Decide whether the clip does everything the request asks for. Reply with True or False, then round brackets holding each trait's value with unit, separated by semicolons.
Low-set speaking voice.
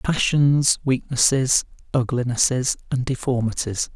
True (130 Hz)